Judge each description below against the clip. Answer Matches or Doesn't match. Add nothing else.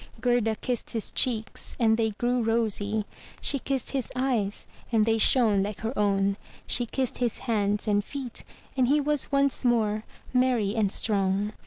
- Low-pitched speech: Doesn't match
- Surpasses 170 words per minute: Doesn't match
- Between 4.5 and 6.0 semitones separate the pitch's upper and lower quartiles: Doesn't match